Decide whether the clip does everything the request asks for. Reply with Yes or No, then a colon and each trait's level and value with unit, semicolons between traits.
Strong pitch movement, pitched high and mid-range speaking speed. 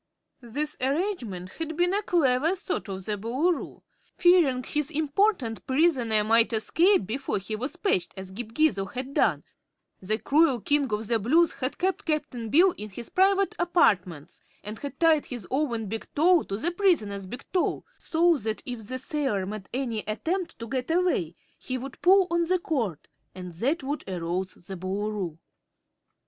Yes: wide, 7.6 semitones; very high, 255 Hz; average, 170 wpm